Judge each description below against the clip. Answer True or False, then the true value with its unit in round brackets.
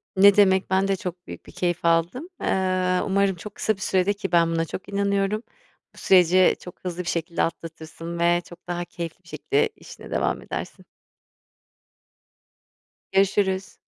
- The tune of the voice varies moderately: False (2.3 semitones)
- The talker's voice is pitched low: False (185 Hz)